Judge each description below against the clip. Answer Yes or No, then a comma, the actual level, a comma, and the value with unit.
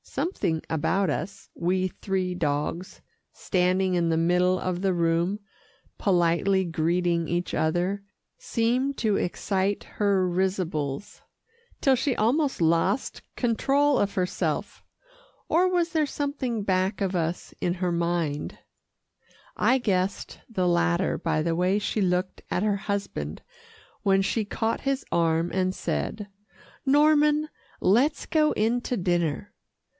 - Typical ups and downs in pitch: Yes, average, 4.4 semitones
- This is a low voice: No, high, 190 Hz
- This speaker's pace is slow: Yes, slow, 130 wpm